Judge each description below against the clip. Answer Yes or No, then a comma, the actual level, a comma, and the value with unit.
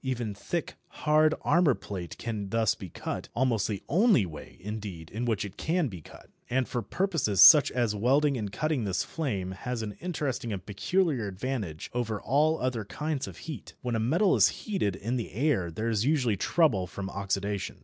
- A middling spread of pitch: No, wide, 6.5 semitones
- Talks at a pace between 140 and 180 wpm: No, average, 190 wpm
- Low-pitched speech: Yes, low, 115 Hz